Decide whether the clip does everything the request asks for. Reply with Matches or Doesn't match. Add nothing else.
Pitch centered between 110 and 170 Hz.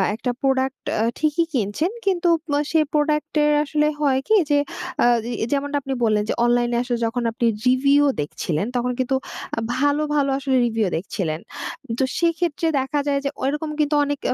Doesn't match